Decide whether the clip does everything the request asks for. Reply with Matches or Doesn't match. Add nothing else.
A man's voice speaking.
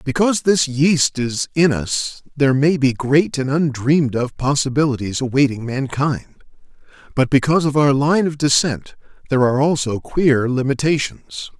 Matches